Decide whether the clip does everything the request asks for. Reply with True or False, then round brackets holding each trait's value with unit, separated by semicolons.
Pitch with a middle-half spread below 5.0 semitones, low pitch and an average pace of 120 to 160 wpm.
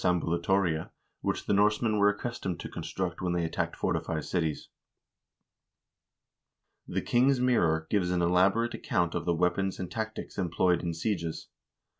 True (3.4 semitones; 90 Hz; 145 wpm)